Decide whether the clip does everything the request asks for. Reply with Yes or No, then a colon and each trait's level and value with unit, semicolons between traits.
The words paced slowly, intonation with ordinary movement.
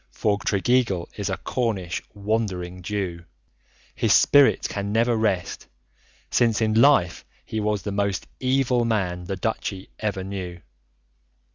Yes: slow, 130 wpm; average, 3.3 semitones